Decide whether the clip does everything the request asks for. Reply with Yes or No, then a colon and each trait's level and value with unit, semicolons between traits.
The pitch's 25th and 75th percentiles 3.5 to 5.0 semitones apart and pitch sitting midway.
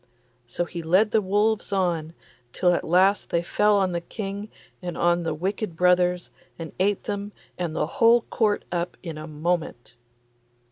No: average, 3.1 semitones; medium, 180 Hz